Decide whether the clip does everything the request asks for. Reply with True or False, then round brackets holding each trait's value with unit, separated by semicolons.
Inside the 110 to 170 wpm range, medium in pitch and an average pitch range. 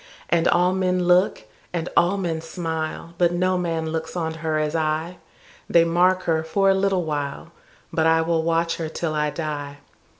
False (165 wpm; 165 Hz; 1.9 semitones)